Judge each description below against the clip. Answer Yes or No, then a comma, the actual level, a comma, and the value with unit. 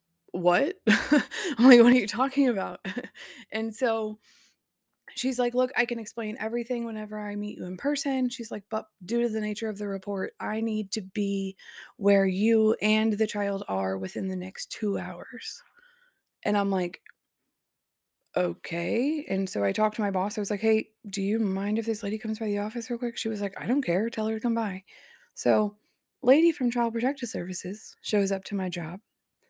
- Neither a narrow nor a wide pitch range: Yes, average, 3.4 semitones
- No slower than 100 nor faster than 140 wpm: No, average, 195 wpm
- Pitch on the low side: No, high, 215 Hz